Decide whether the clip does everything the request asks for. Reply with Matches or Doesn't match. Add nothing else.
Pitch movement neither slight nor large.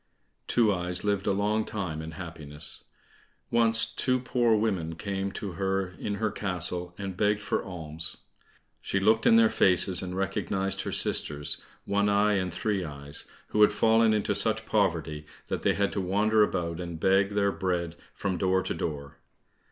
Matches